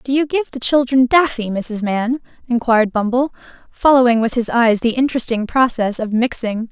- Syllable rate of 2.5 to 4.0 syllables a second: No, 5.2 syllables/s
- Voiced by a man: No, female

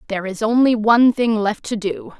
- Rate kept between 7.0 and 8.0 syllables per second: No, 5.6 syllables/s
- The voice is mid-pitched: No, high, 220 Hz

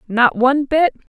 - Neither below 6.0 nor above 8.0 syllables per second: No, 5.1 syllables/s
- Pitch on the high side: Yes, very high, 265 Hz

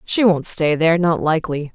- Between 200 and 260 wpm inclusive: Yes, fast, 205 wpm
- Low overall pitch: No, medium, 165 Hz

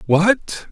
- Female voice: No, male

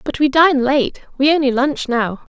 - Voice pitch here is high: Yes, very high, 270 Hz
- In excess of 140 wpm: Yes, fast, 205 wpm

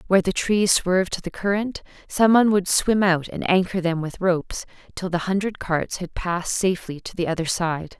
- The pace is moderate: No, fast, 210 wpm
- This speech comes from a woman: Yes, female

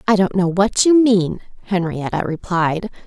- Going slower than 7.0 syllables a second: Yes, 4.5 syllables/s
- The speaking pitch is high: Yes, high, 195 Hz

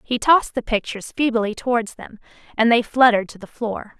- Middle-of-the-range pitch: No, high, 230 Hz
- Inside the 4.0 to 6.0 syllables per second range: Yes, 5.8 syllables/s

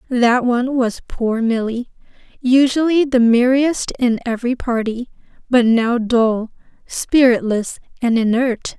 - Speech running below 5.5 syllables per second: Yes, 4.0 syllables/s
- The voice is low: No, high, 245 Hz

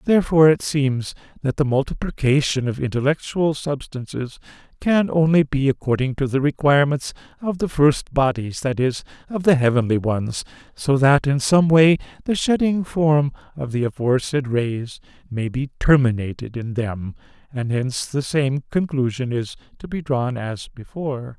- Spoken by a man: Yes, male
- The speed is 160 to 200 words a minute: No, average, 150 wpm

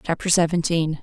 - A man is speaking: No, female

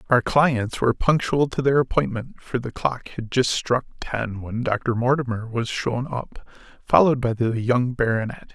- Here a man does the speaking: Yes, male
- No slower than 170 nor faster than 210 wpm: Yes, average, 175 wpm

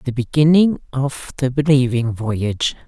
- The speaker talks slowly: Yes, slow, 125 wpm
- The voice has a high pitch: No, low, 135 Hz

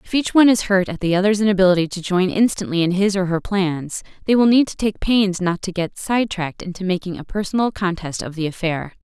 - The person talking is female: Yes, female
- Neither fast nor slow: No, fast, 230 wpm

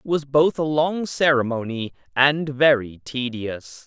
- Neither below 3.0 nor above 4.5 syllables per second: Yes, 3.9 syllables/s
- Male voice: Yes, male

